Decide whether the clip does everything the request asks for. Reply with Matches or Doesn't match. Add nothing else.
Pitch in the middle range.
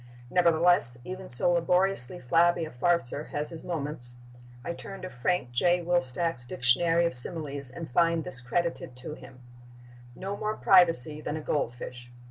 Matches